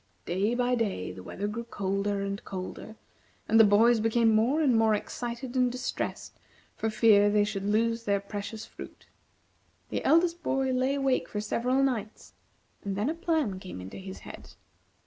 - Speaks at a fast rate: No, average, 170 wpm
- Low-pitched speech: No, high, 220 Hz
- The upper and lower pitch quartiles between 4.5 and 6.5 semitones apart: No, average, 3.7 semitones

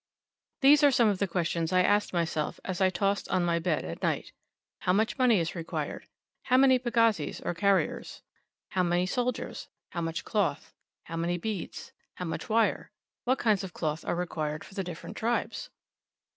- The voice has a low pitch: No, medium, 185 Hz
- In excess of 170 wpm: Yes, average, 180 wpm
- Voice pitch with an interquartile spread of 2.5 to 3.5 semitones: No, average, 4.8 semitones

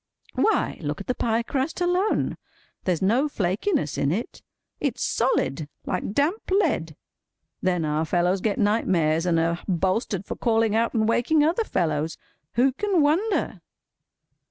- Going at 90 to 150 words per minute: Yes, average, 140 wpm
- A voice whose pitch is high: Yes, high, 215 Hz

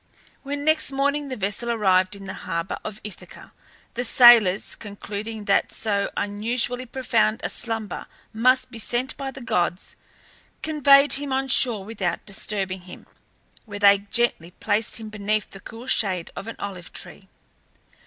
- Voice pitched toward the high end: Yes, high, 220 Hz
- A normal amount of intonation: Yes, average, 4.1 semitones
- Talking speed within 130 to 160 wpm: Yes, average, 155 wpm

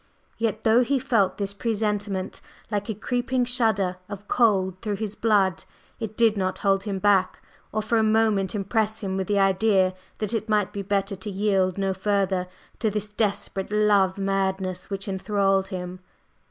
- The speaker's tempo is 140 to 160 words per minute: No, average, 170 wpm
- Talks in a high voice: Yes, high, 200 Hz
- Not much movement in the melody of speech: Yes, narrow, 2.1 semitones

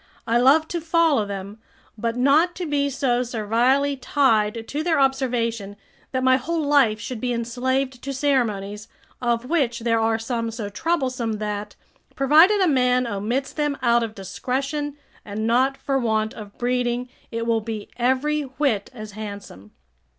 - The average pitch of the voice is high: Yes, high, 245 Hz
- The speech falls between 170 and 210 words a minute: No, average, 160 wpm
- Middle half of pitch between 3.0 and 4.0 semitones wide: Yes, average, 3.7 semitones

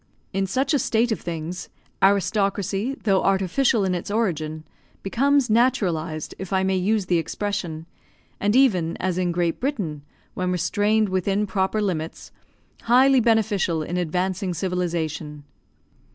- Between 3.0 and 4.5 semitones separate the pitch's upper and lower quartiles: Yes, average, 3.8 semitones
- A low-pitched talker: No, high, 190 Hz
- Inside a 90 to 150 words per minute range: Yes, slow, 135 wpm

